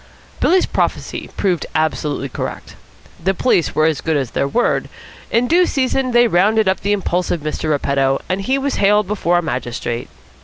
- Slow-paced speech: No, average, 170 wpm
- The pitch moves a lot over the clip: Yes, wide, 7.0 semitones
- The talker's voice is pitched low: No, medium, 180 Hz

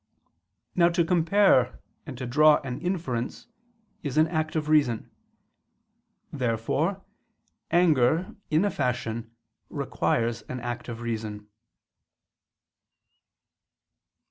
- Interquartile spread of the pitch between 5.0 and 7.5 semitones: Yes, wide, 5.5 semitones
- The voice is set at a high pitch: No, medium, 140 Hz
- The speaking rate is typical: No, slow, 95 wpm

